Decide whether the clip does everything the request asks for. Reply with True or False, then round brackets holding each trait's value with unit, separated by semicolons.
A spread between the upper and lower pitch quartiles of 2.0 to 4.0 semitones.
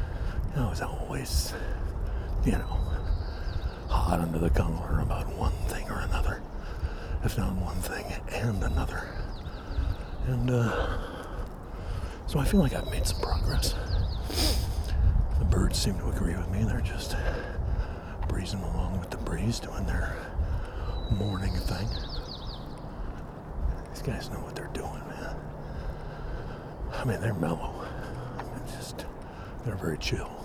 True (3.3 semitones)